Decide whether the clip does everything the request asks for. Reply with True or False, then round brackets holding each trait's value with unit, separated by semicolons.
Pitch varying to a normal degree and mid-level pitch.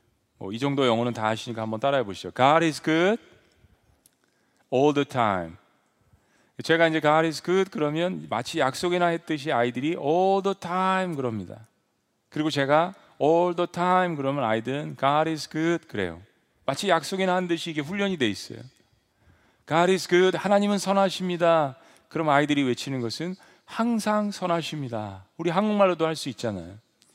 False (6.7 semitones; 155 Hz)